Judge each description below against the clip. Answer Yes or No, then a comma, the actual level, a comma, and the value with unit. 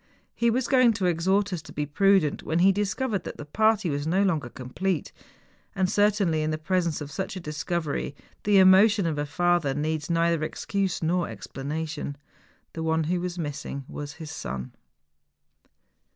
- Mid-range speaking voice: Yes, medium, 170 Hz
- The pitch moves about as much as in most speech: Yes, average, 4.3 semitones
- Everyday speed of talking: Yes, average, 165 wpm